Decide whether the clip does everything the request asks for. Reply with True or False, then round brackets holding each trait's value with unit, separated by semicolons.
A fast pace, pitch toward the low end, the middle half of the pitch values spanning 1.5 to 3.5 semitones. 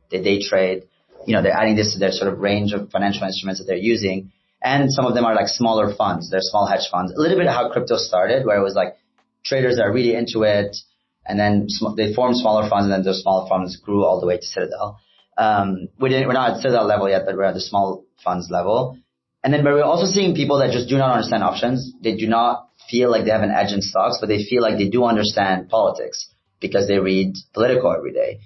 False (250 wpm; 105 Hz; 3.9 semitones)